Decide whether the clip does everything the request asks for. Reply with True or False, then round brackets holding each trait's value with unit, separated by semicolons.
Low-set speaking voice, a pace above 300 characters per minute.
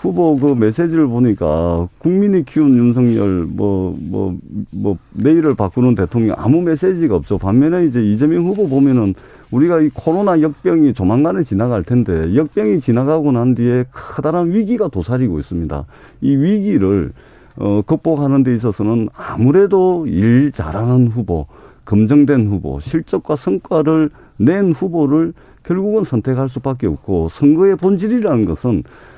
True (130 Hz; 315 characters per minute)